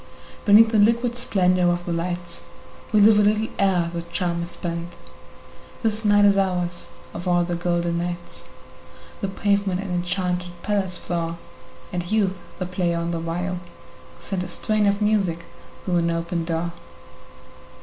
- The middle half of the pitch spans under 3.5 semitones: Yes, average, 2.7 semitones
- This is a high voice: No, medium, 180 Hz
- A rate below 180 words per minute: Yes, average, 160 wpm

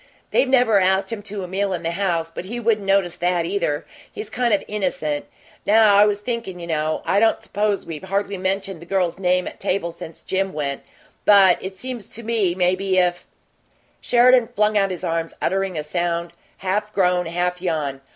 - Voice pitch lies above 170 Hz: Yes, high, 190 Hz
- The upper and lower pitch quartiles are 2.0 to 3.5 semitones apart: Yes, average, 2.9 semitones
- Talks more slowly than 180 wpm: No, average, 200 wpm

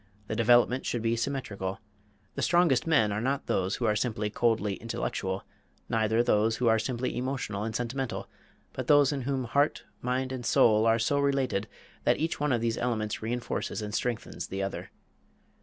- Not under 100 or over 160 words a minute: No, average, 180 wpm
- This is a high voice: No, low, 115 Hz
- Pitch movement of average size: Yes, average, 3.3 semitones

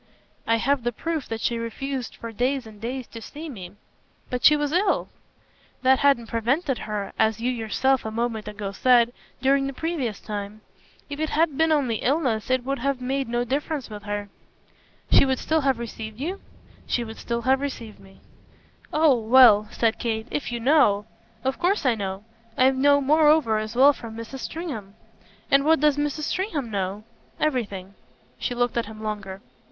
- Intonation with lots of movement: No, average, 4.2 semitones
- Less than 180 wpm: No, average, 185 wpm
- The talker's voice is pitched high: Yes, high, 245 Hz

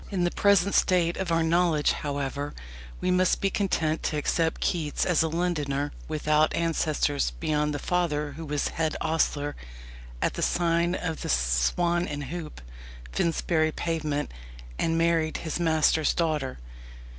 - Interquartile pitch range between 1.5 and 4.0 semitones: Yes, narrow, 2.6 semitones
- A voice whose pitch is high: No, medium, 160 Hz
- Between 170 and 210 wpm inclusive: No, average, 145 wpm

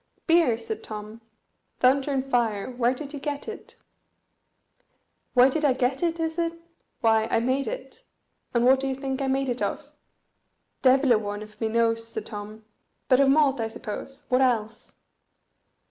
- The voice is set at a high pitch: Yes, very high, 255 Hz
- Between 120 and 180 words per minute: Yes, average, 175 wpm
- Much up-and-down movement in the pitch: No, average, 3.3 semitones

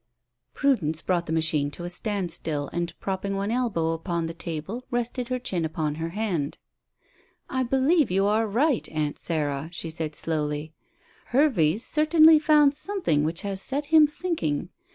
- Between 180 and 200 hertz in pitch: Yes, medium, 185 Hz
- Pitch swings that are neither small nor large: No, wide, 8.1 semitones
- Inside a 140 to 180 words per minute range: Yes, average, 160 wpm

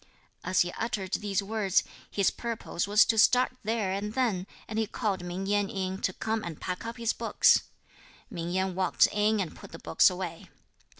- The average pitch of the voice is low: No, high, 200 Hz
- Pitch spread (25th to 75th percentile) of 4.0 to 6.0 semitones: No, average, 2.9 semitones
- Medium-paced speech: Yes, average, 190 wpm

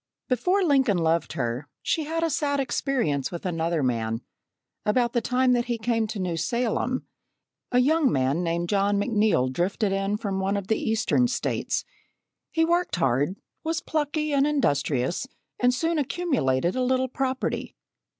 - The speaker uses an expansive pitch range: Yes, wide, 7.8 semitones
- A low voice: No, high, 225 Hz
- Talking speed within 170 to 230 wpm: No, average, 160 wpm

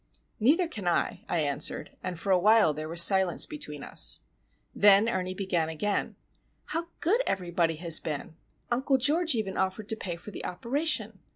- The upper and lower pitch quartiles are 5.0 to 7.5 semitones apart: Yes, wide, 5.4 semitones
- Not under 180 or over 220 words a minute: No, average, 165 wpm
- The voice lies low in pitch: No, high, 190 Hz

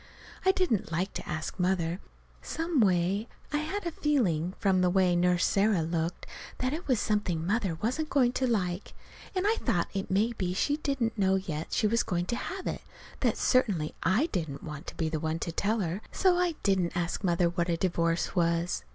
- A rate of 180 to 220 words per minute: Yes, average, 200 wpm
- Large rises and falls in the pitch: Yes, wide, 5.9 semitones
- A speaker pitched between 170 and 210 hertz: Yes, high, 190 Hz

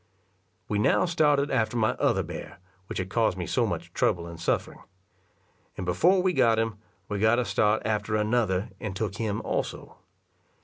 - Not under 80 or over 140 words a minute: No, average, 175 wpm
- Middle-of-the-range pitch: No, low, 110 Hz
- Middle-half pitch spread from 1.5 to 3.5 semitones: Yes, average, 3.1 semitones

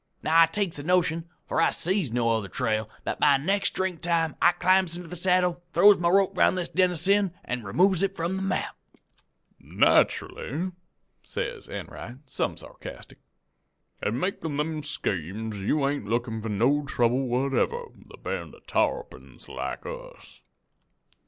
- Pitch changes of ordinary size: No, wide, 6.8 semitones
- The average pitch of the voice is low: No, medium, 165 Hz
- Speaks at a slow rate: No, average, 165 wpm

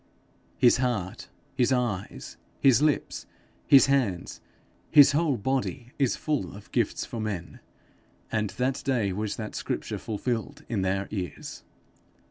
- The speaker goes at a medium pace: No, slow, 130 wpm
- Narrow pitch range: No, average, 5.0 semitones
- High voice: No, low, 120 Hz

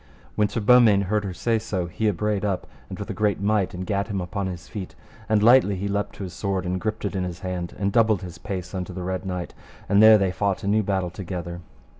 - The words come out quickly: Yes, fast, 245 wpm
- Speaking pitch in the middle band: No, low, 100 Hz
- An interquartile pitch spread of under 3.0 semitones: Yes, narrow, 2.4 semitones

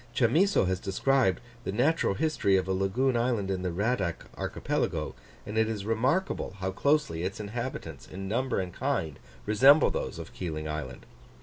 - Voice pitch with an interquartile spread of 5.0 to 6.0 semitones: Yes, wide, 5.4 semitones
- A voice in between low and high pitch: No, low, 100 Hz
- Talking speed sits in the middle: Yes, average, 165 wpm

